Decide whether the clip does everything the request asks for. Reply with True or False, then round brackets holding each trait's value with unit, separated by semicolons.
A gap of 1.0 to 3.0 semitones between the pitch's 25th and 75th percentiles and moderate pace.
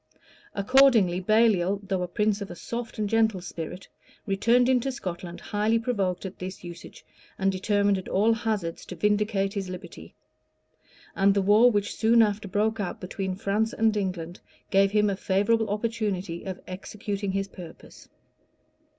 True (2.7 semitones; 155 wpm)